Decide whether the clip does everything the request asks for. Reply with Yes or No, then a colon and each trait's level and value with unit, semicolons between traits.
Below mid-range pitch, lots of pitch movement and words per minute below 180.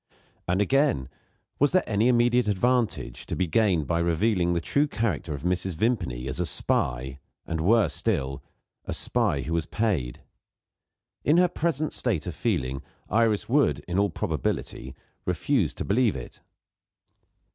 Yes: very low, 95 Hz; wide, 6.9 semitones; average, 150 wpm